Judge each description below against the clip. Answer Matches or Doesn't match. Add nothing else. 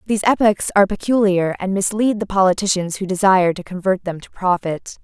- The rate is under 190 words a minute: Matches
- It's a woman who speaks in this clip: Matches